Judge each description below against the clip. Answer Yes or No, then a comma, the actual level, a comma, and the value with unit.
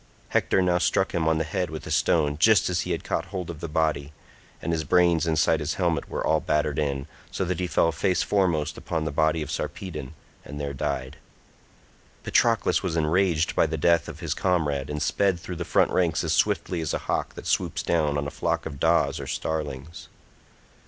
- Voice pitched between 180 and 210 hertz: No, very low, 80 Hz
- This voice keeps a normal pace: No, fast, 210 wpm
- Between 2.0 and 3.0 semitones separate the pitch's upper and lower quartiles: Yes, average, 2.7 semitones